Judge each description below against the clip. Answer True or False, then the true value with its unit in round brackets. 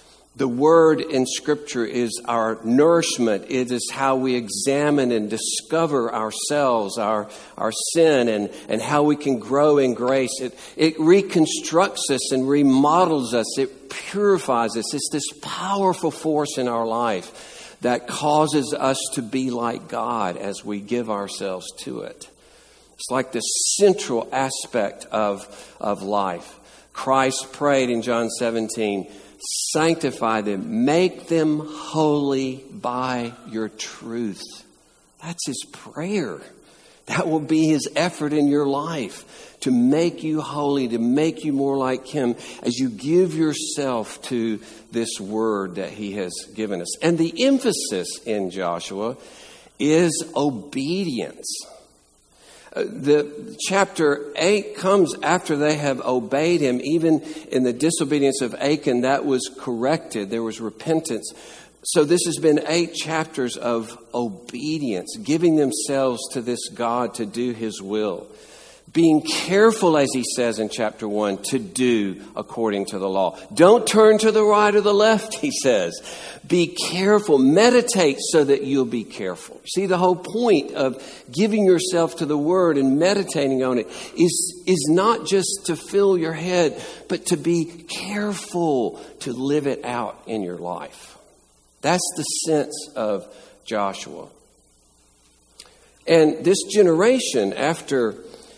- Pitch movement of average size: False (5.9 semitones)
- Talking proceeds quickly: False (140 wpm)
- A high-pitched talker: False (140 Hz)